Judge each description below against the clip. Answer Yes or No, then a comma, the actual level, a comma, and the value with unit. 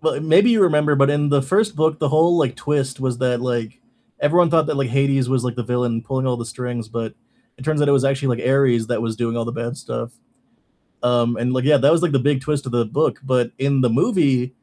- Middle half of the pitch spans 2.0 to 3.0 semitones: No, average, 3.4 semitones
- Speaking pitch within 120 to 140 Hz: Yes, low, 135 Hz